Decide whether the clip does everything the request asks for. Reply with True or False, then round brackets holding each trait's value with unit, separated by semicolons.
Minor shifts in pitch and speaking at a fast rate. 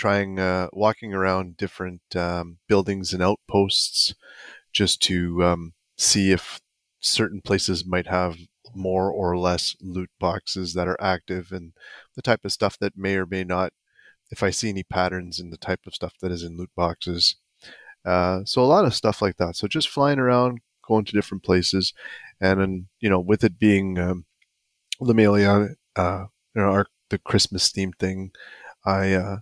False (1.9 semitones; 175 wpm)